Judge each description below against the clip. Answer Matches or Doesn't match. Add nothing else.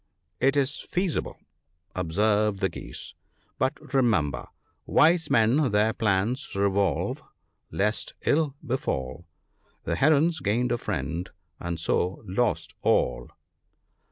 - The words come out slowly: Matches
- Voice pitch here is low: Matches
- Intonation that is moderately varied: Doesn't match